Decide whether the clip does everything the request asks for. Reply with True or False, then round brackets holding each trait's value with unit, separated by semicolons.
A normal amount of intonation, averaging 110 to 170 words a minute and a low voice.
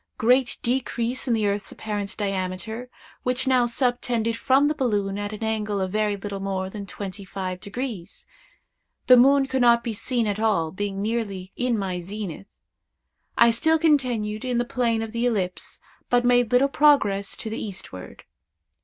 False (3.7 semitones; 165 wpm; 220 Hz)